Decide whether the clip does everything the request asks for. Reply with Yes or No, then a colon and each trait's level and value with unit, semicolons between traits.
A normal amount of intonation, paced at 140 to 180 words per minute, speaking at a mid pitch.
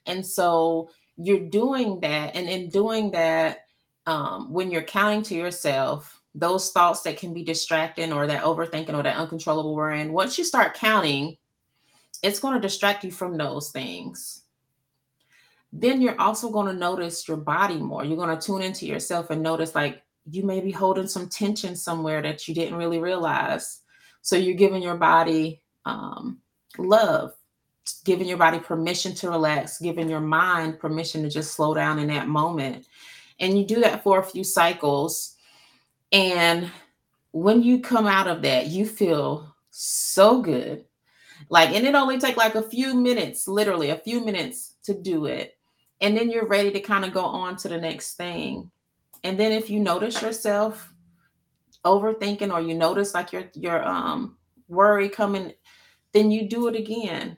Yes: average, 4.1 semitones; average, 170 wpm; medium, 180 Hz